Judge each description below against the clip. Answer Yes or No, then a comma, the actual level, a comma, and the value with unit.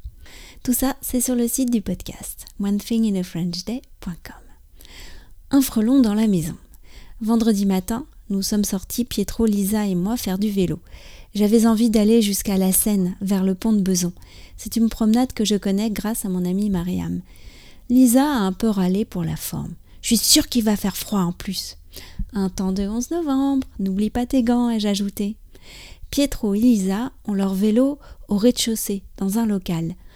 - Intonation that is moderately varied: Yes, average, 3.4 semitones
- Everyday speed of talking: Yes, average, 180 wpm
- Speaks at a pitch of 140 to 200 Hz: No, high, 210 Hz